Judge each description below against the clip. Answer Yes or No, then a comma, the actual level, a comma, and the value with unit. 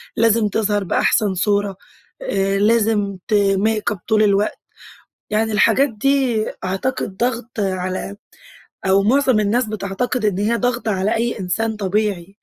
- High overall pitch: Yes, high, 210 Hz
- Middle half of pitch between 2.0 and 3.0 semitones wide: Yes, narrow, 2.6 semitones